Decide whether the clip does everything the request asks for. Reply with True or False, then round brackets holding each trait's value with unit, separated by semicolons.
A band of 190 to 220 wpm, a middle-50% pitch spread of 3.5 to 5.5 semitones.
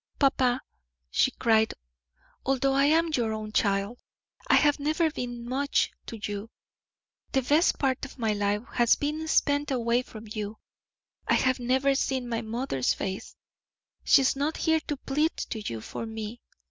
False (160 wpm; 4.2 semitones)